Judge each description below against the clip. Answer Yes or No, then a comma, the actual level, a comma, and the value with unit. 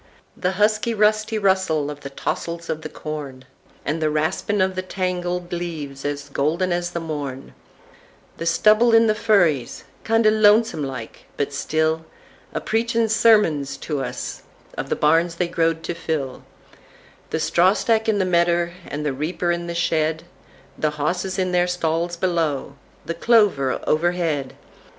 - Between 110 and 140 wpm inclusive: Yes, slow, 135 wpm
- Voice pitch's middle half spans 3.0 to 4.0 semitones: Yes, average, 3.7 semitones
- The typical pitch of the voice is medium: Yes, medium, 170 Hz